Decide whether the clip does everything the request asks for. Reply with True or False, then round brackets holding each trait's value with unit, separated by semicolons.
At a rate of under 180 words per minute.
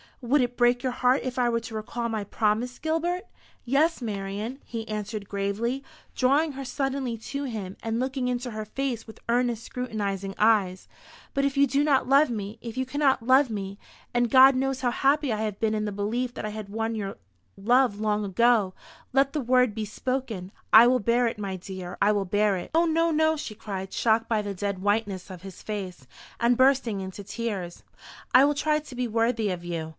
False (205 wpm)